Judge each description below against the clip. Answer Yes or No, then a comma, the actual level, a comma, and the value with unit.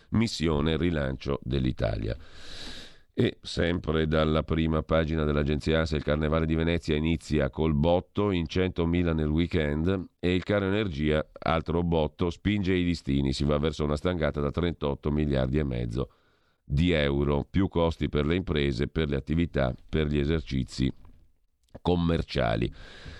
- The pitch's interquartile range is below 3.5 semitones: Yes, average, 2.7 semitones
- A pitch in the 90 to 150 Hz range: No, very low, 80 Hz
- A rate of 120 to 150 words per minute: Yes, average, 140 wpm